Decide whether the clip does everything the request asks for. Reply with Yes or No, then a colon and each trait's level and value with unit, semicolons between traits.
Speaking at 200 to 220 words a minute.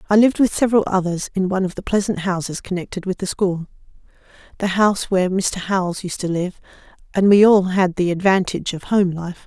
Yes: fast, 205 wpm